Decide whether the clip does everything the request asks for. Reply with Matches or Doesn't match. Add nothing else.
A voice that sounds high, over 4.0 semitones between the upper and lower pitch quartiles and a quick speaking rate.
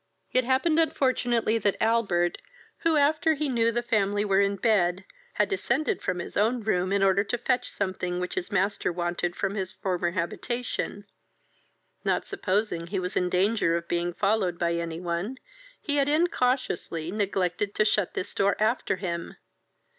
Doesn't match